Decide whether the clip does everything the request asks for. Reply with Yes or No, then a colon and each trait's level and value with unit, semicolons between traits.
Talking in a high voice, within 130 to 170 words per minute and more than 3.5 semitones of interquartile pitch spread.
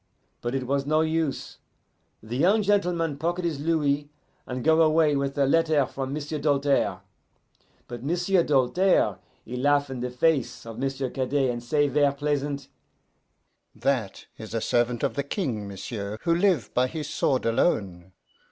No: medium, 140 Hz; average, 160 wpm; average, 4.0 semitones